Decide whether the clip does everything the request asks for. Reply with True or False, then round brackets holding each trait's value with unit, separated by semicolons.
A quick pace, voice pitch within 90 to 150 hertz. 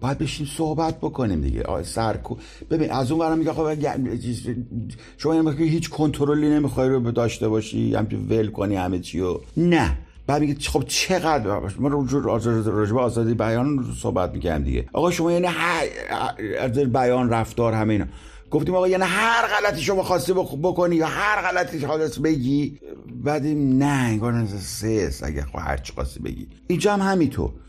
True (170 wpm; 135 Hz)